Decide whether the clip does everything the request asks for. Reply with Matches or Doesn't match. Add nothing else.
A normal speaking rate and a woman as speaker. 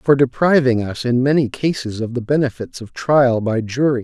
Doesn't match